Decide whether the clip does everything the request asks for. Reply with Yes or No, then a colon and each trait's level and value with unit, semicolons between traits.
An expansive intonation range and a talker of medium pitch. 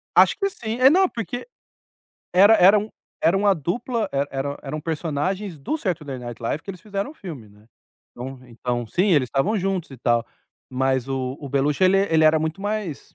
Yes: wide, 7.0 semitones; medium, 160 Hz